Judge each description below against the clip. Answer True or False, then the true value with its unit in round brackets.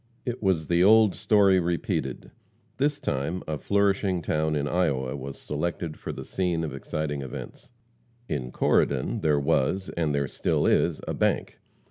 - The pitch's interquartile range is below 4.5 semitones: False (4.8 semitones)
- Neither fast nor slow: True (155 wpm)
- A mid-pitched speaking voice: False (80 Hz)